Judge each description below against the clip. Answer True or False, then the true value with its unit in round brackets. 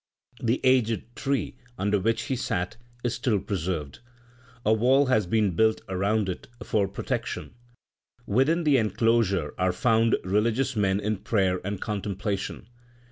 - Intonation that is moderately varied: True (3.4 semitones)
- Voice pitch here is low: True (105 Hz)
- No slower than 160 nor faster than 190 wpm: False (135 wpm)